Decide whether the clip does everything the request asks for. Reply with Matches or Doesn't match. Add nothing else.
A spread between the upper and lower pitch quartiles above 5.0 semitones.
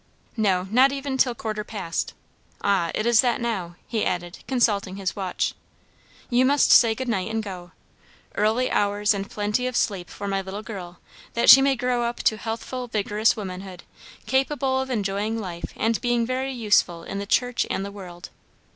Doesn't match